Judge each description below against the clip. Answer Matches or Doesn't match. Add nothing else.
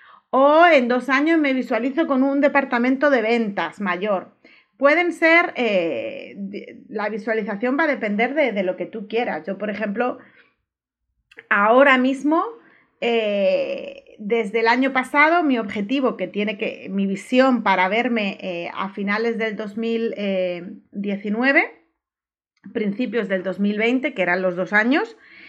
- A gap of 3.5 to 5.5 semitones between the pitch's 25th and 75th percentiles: Matches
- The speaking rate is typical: Matches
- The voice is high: Matches